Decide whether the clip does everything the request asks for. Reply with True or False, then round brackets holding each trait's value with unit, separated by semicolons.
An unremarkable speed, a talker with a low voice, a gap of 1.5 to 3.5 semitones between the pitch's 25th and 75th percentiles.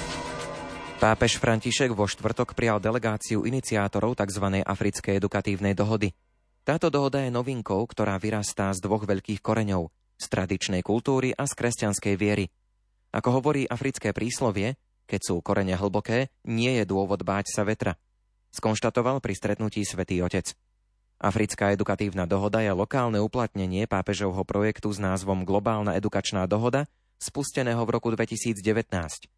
True (130 wpm; 105 Hz; 2.7 semitones)